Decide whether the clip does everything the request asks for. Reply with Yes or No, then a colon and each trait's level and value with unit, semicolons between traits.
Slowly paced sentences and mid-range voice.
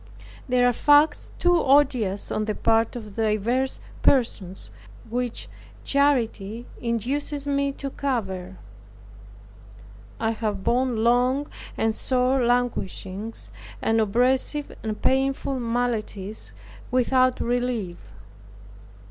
No: slow, 95 wpm; high, 245 Hz